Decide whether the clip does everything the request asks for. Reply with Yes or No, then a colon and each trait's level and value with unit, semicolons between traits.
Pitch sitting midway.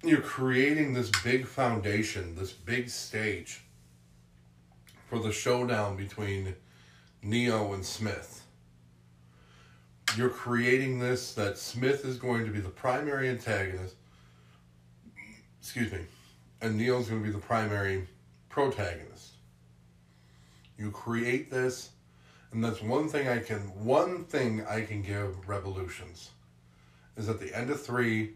No: low, 100 Hz